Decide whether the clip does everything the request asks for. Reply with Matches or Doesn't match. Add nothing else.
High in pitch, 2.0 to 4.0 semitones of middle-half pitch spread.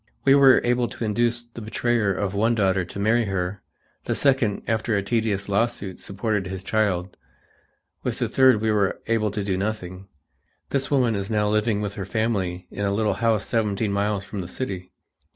Doesn't match